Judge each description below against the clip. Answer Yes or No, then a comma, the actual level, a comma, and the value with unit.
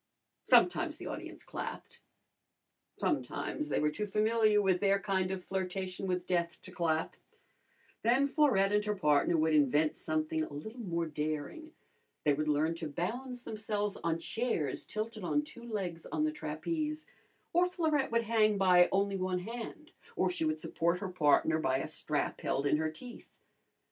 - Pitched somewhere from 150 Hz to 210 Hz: Yes, high, 190 Hz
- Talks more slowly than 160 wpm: No, average, 165 wpm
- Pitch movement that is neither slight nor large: No, wide, 6.2 semitones